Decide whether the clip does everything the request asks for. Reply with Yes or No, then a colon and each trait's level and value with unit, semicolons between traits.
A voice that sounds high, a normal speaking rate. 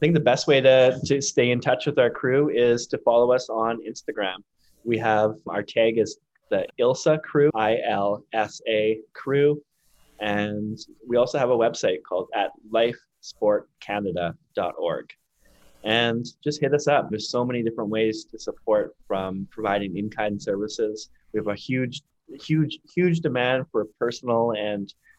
No: low, 120 Hz; average, 160 wpm